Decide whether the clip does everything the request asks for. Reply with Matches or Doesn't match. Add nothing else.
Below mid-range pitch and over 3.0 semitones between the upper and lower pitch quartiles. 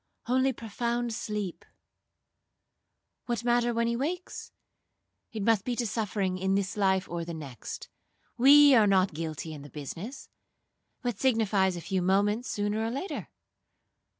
Doesn't match